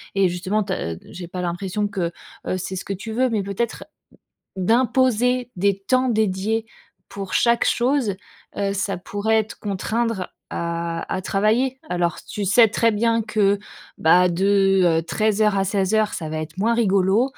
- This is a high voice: Yes, high, 200 Hz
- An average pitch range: Yes, average, 3.2 semitones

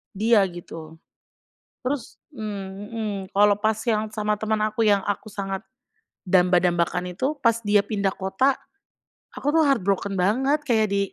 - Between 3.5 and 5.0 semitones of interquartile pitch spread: No, average, 2.7 semitones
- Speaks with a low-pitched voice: No, high, 210 Hz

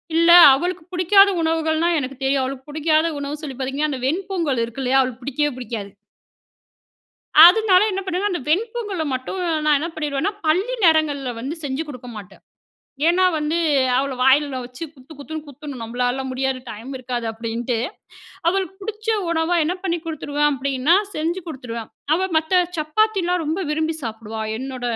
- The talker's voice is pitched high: Yes, very high, 300 Hz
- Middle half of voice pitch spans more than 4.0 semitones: Yes, average, 4.9 semitones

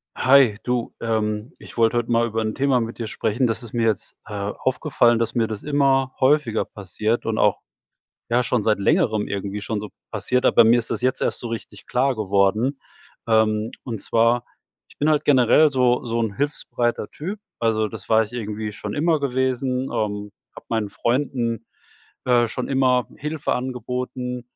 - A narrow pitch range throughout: No, average, 3.0 semitones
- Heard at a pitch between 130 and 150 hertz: No, low, 120 Hz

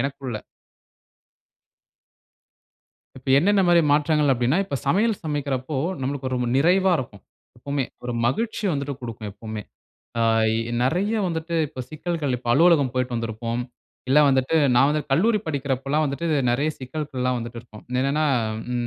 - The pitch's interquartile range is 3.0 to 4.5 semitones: Yes, average, 3.9 semitones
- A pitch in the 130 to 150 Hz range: Yes, medium, 140 Hz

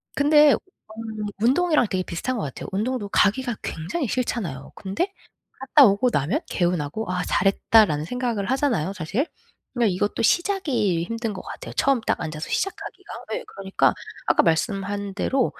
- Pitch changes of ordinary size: No, wide, 5.7 semitones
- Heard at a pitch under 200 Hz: No, high, 215 Hz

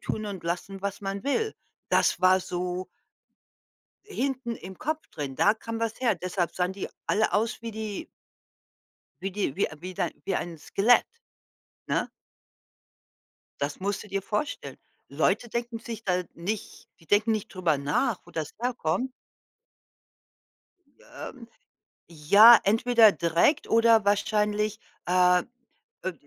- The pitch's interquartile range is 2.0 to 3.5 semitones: No, average, 4.0 semitones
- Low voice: No, high, 205 Hz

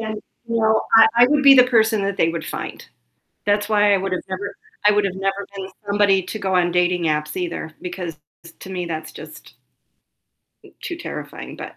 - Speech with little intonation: No, average, 3.4 semitones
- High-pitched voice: Yes, high, 195 Hz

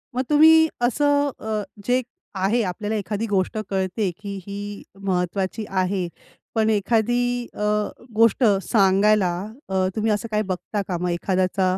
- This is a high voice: Yes, high, 205 Hz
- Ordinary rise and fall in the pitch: Yes, average, 3.3 semitones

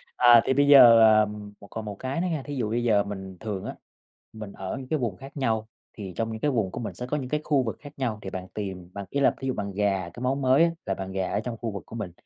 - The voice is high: No, low, 110 Hz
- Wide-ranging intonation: No, average, 4.7 semitones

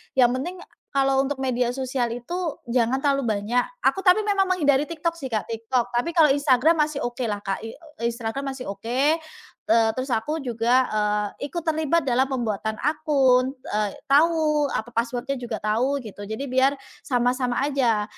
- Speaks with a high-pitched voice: Yes, very high, 260 Hz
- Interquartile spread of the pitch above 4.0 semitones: No, average, 3.6 semitones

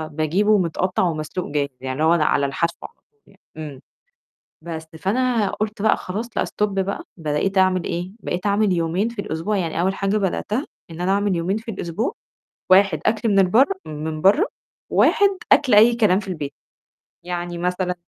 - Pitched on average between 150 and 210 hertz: Yes, medium, 185 Hz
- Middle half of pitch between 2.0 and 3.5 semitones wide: No, average, 3.9 semitones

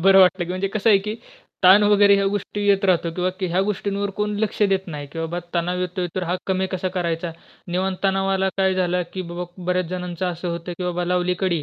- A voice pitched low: No, medium, 185 Hz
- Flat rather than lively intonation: Yes, narrow, 1.6 semitones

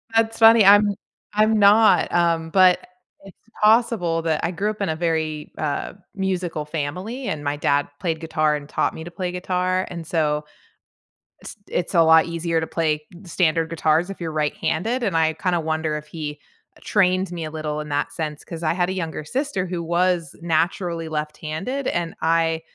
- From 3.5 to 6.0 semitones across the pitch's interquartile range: No, average, 2.9 semitones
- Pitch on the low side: No, medium, 165 Hz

